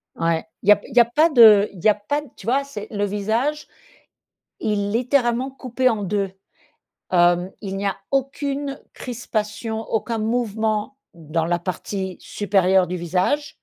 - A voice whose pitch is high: Yes, high, 215 Hz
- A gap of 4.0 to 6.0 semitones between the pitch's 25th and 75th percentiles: Yes, average, 4.4 semitones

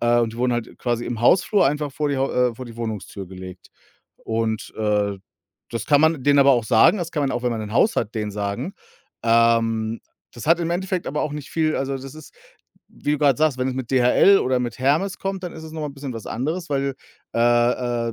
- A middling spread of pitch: Yes, average, 4.6 semitones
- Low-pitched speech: Yes, low, 130 Hz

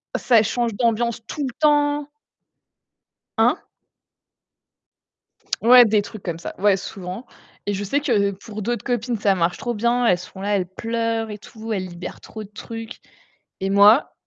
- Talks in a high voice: Yes, high, 220 Hz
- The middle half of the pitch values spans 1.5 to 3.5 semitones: Yes, average, 3.1 semitones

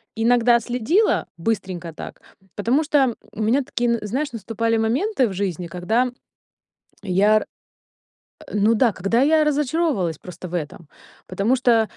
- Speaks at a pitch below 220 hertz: No, high, 225 Hz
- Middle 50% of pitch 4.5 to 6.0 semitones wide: Yes, average, 4.8 semitones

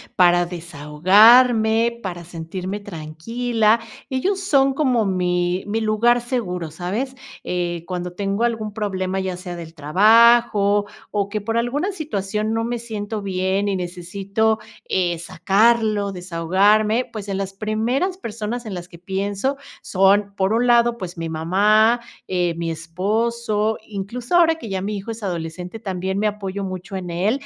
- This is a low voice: No, high, 200 Hz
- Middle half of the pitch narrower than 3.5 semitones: No, average, 4.0 semitones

